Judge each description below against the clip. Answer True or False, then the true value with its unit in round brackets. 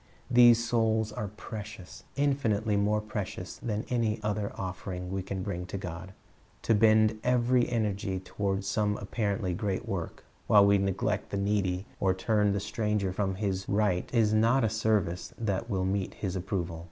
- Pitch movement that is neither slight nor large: False (2.3 semitones)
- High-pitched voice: False (105 Hz)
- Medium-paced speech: True (165 wpm)